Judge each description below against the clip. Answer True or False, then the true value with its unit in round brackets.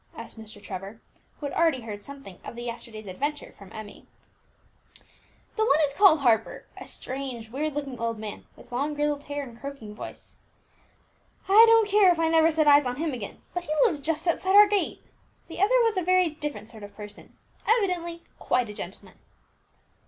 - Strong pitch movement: True (6.6 semitones)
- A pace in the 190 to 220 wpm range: True (195 wpm)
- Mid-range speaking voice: False (285 Hz)